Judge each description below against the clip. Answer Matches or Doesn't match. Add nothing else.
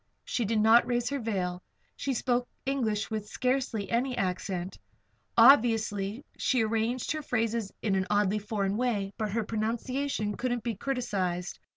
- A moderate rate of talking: Matches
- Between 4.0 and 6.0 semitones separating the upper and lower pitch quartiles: Doesn't match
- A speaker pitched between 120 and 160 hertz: Doesn't match